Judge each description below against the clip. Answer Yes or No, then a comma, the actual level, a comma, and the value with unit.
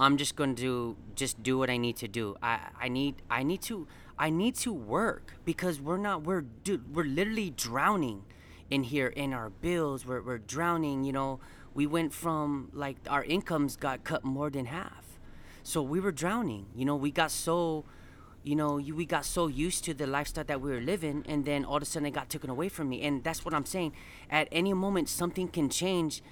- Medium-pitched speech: Yes, medium, 145 Hz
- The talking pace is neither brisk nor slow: No, fast, 220 wpm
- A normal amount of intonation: Yes, average, 3.9 semitones